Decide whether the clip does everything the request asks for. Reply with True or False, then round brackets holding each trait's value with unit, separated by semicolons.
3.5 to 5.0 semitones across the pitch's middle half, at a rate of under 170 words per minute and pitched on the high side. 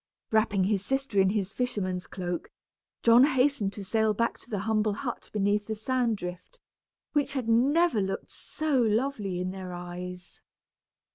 True (4.6 semitones; 155 wpm; 215 Hz)